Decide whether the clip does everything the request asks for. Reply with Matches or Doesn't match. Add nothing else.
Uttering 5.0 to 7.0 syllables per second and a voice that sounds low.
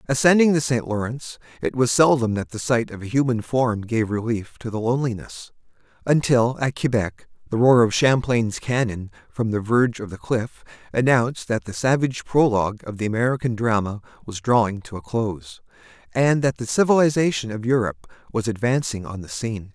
Matches